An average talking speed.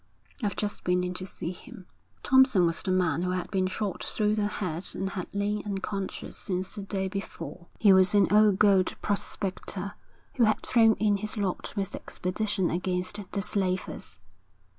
Yes: average, 180 wpm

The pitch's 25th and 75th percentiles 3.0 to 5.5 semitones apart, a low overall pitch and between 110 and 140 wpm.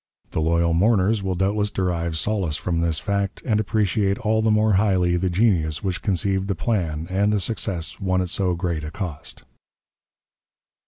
No: average, 3.5 semitones; very low, 95 Hz; average, 170 wpm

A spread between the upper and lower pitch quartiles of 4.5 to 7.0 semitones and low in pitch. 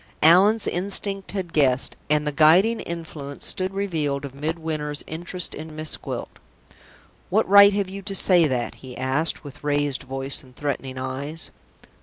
No: average, 4.8 semitones; medium, 155 Hz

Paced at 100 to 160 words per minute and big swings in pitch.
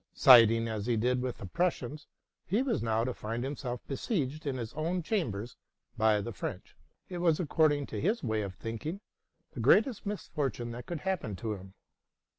No: average, 180 wpm; wide, 6.4 semitones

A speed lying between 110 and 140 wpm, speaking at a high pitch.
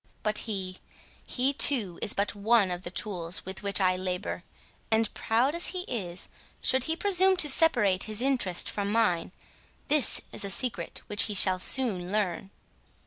No: average, 165 wpm; high, 210 Hz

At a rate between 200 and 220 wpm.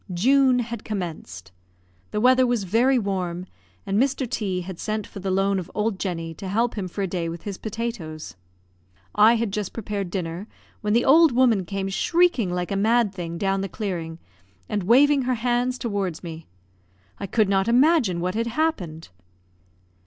No: average, 175 wpm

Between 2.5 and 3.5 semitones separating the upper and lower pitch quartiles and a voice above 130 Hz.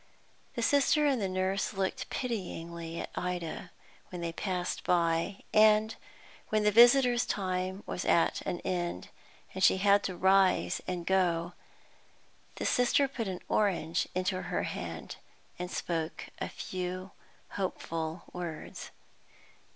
Yes: average, 3.2 semitones; medium, 185 Hz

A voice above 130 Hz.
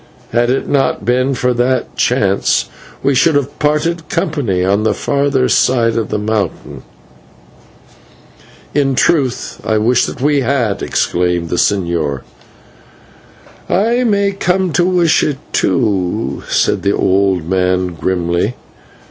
No: low, 125 Hz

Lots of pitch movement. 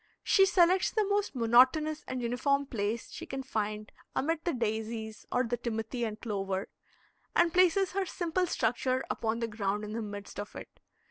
Yes: wide, 6.7 semitones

